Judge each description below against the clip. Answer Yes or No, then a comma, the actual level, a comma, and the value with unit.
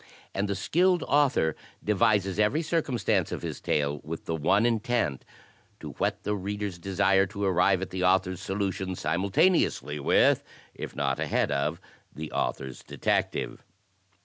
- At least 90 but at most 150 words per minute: Yes, average, 145 wpm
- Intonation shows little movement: No, average, 3.8 semitones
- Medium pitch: No, very low, 95 Hz